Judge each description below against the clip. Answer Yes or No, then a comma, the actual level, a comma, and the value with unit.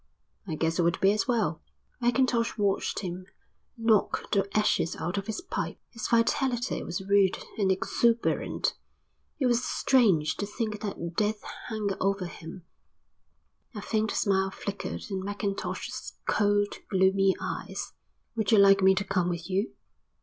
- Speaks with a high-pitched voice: Yes, high, 200 Hz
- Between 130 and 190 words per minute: Yes, average, 150 wpm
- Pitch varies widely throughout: No, narrow, 2.6 semitones